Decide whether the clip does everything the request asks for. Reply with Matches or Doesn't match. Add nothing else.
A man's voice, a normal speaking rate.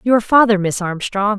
Doesn't match